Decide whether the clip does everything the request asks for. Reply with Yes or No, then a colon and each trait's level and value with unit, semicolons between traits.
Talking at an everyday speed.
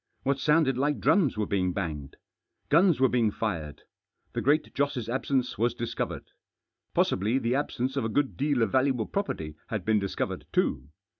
Yes: average, 170 wpm